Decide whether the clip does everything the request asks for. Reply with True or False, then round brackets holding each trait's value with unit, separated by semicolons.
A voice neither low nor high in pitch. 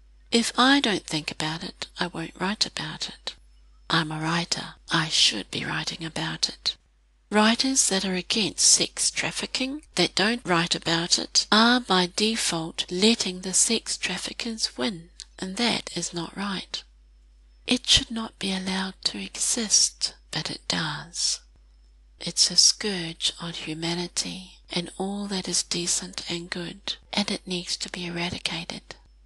True (180 Hz)